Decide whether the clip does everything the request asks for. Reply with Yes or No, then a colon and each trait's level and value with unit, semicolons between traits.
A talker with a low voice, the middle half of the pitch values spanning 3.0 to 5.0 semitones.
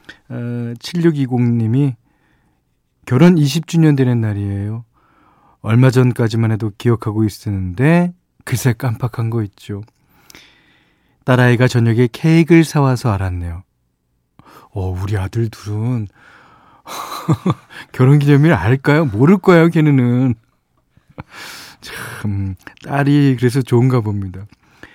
Yes: low, 120 Hz; average, 4.5 semitones